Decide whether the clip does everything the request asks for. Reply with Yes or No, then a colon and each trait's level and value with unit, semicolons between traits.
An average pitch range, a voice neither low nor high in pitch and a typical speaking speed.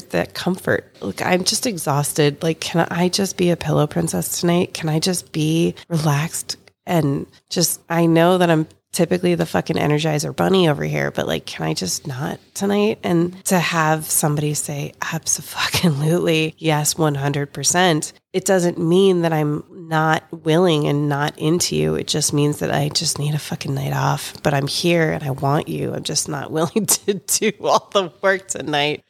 Yes: average, 3.1 semitones; medium, 160 Hz; average, 180 wpm